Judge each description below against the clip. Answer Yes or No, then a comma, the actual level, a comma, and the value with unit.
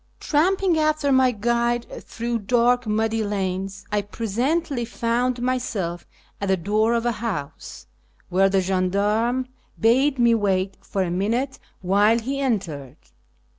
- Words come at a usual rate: No, slow, 130 wpm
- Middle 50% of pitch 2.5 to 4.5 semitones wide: Yes, average, 4.1 semitones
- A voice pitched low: No, high, 225 Hz